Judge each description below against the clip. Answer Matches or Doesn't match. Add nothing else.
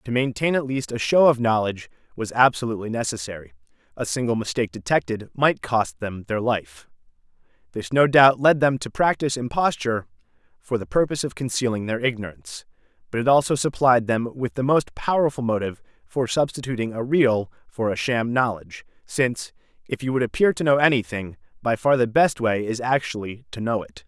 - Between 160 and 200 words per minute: Matches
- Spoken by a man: Matches